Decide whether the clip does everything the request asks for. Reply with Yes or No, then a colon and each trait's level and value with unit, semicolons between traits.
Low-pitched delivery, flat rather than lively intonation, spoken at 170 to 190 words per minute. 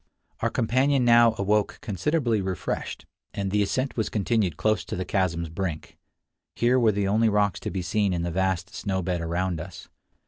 No: low, 100 Hz; average, 3.5 semitones; average, 180 wpm